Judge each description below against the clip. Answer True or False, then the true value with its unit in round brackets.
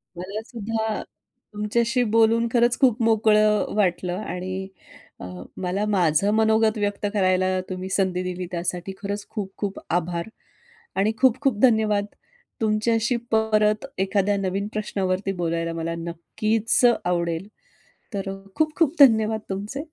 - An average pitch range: True (3.0 semitones)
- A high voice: True (205 Hz)